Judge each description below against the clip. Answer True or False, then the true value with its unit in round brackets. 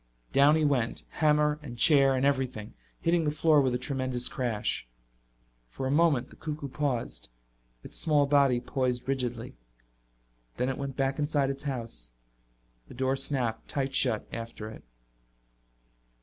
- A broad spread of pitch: False (2.9 semitones)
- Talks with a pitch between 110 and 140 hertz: True (135 Hz)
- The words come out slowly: False (150 wpm)